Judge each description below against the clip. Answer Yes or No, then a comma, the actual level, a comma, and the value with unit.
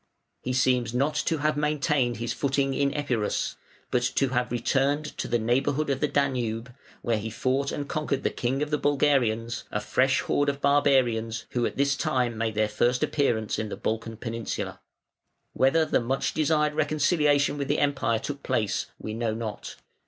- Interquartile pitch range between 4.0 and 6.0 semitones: No, average, 3.6 semitones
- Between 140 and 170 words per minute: No, average, 180 wpm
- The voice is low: Yes, low, 130 Hz